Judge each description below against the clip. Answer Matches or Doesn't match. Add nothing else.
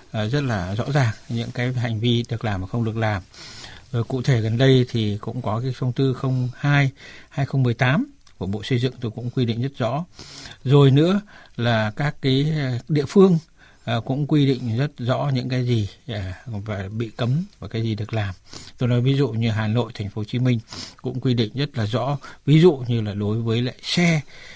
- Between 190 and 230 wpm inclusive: Matches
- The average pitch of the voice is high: Doesn't match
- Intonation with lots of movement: Doesn't match